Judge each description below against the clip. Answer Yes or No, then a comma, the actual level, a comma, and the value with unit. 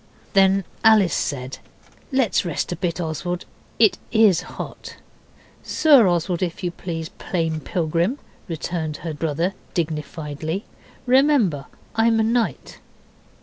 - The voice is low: No, medium, 175 Hz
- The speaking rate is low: Yes, slow, 115 wpm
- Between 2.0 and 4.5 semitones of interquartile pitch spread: No, average, 5.2 semitones